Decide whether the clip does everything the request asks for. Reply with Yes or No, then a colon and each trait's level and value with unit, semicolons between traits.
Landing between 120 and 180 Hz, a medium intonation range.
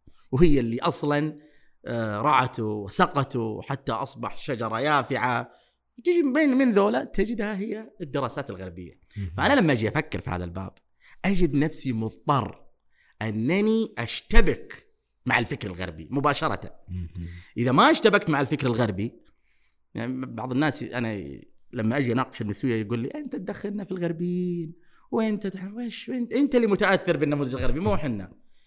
No: medium, 140 Hz; wide, 9.0 semitones